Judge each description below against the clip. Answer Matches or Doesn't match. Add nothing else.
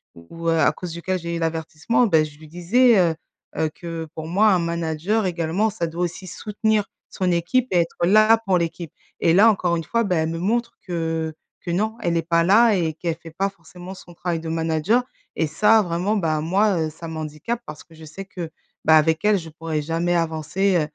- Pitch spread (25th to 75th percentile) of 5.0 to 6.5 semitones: Doesn't match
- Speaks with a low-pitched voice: Doesn't match